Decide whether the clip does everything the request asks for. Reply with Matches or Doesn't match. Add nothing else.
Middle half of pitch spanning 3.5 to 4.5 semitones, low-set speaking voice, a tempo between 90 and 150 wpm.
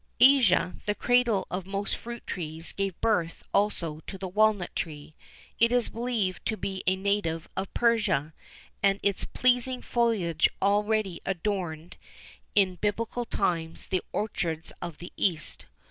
Doesn't match